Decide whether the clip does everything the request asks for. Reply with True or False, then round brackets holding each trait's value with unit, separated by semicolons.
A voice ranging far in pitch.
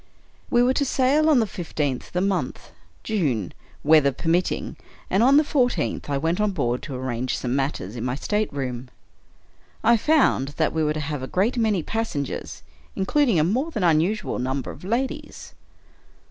True (8.5 semitones)